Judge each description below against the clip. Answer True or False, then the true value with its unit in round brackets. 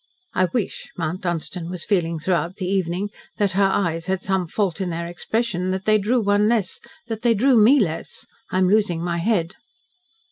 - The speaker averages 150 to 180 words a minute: False (190 wpm)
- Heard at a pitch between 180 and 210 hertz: True (190 Hz)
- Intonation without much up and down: False (3.3 semitones)